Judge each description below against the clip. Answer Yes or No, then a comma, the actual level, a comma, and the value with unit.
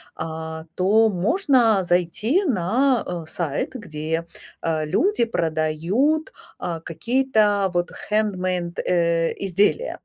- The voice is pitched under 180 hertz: No, medium, 185 Hz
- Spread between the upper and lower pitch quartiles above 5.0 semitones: Yes, wide, 5.6 semitones